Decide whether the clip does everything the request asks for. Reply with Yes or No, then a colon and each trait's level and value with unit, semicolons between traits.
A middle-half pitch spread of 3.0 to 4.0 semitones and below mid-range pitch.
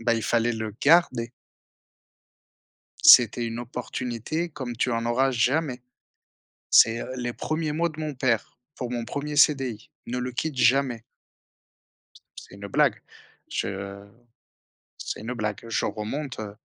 Yes: average, 3.5 semitones; low, 120 Hz